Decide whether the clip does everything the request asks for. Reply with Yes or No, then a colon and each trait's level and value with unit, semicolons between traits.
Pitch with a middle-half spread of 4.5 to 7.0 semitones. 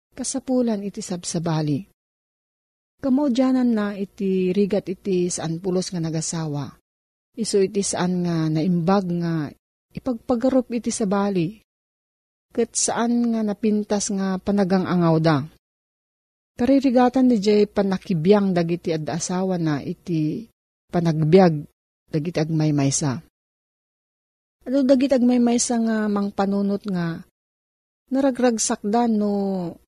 Yes: average, 5.1 semitones